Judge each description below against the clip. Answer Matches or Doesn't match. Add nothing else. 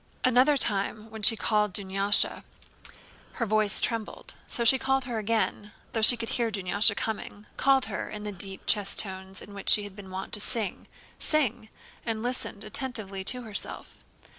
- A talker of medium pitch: Doesn't match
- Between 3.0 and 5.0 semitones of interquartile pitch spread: Doesn't match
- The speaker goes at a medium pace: Matches